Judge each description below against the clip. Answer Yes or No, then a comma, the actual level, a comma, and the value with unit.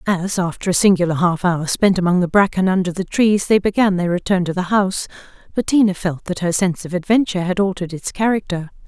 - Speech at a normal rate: No, fast, 210 wpm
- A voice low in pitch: No, medium, 185 Hz